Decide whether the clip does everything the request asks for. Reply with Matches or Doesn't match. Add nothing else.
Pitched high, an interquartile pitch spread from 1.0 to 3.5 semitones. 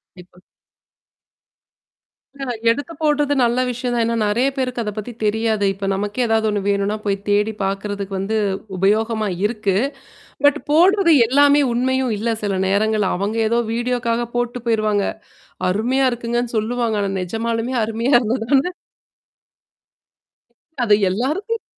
Matches